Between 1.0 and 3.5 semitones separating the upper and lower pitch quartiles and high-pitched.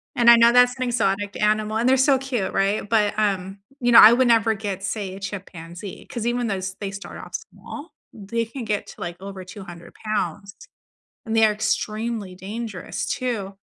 Yes: average, 3.2 semitones; high, 215 Hz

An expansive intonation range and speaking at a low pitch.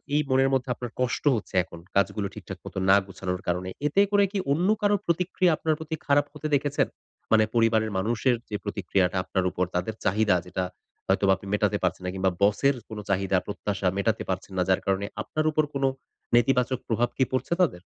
Yes: wide, 5.9 semitones; low, 110 Hz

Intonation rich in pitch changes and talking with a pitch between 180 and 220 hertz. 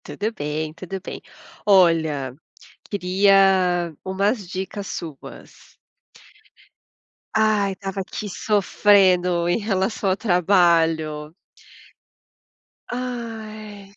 No: average, 3.1 semitones; high, 190 Hz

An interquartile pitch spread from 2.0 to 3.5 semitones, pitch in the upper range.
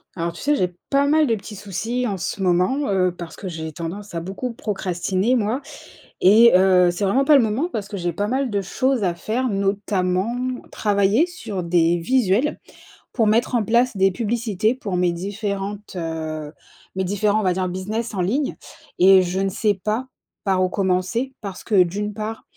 No: average, 3.9 semitones; high, 200 Hz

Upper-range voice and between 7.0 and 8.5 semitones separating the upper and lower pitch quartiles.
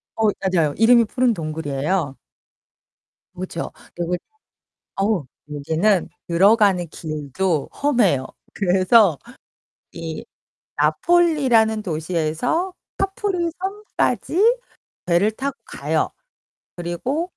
Yes: high, 195 Hz; wide, 7.5 semitones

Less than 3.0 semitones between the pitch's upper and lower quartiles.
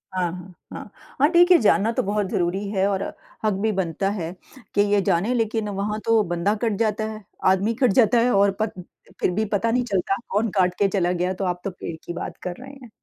No: average, 3.3 semitones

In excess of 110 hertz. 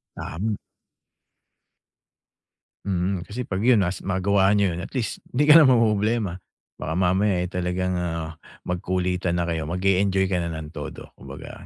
No: very low, 95 Hz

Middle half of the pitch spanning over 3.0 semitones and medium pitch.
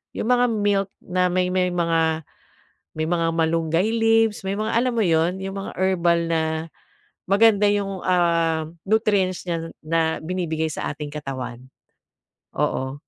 Yes: average, 3.4 semitones; medium, 175 Hz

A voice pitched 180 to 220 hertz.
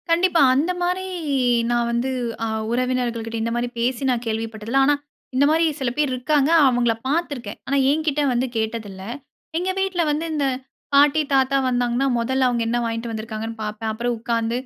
No: high, 245 Hz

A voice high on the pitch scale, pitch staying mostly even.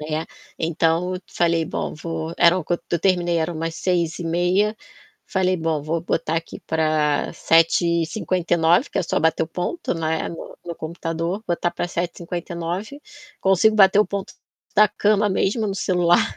No: medium, 170 Hz; narrow, 2.1 semitones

